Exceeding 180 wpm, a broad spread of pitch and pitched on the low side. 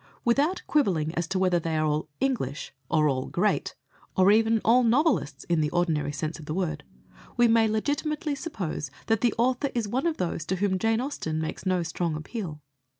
No: average, 195 wpm; wide, 7.2 semitones; high, 190 Hz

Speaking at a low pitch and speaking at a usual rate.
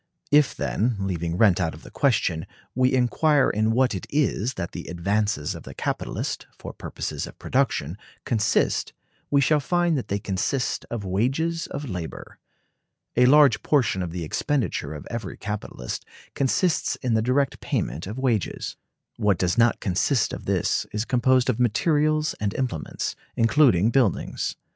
Yes: low, 115 Hz; average, 160 wpm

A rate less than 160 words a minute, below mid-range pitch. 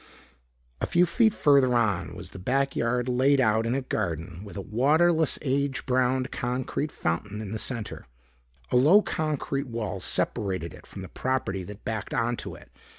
No: average, 165 wpm; low, 125 Hz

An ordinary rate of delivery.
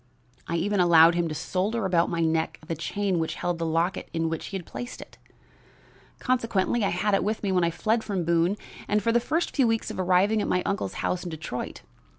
No: fast, 225 wpm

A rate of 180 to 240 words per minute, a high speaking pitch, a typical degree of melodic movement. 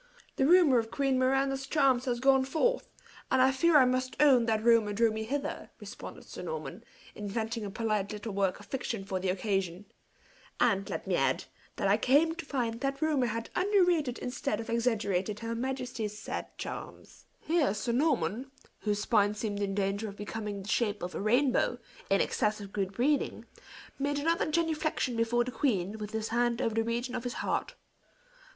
Yes: average, 185 wpm; high, 235 Hz; average, 4.4 semitones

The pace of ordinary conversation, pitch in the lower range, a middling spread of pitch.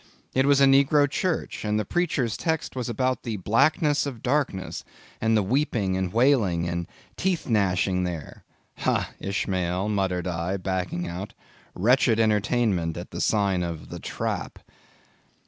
No: average, 145 wpm; low, 105 Hz; wide, 6.0 semitones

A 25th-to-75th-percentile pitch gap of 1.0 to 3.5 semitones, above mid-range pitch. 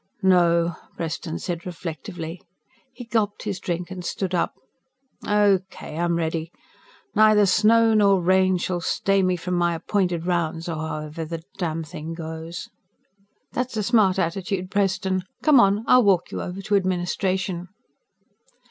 No: average, 2.8 semitones; medium, 180 Hz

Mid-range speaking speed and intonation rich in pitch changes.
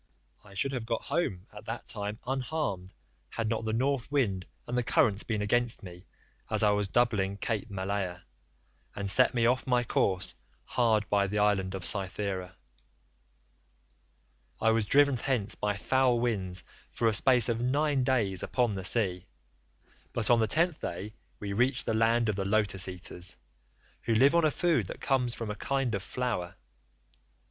No: average, 170 wpm; average, 3.9 semitones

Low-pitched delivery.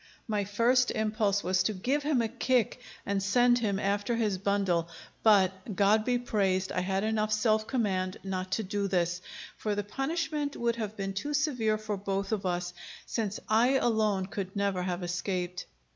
No: high, 205 Hz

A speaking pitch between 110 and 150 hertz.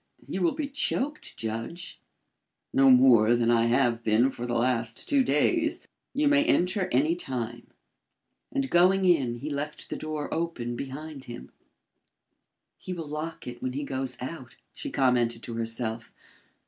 Yes: low, 135 Hz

